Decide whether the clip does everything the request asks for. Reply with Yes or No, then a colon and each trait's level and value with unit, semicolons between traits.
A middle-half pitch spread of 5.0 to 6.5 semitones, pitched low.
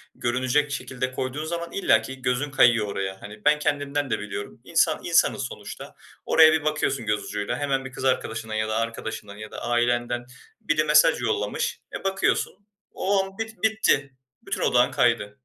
Yes: average, 5.3 semitones; low, 130 Hz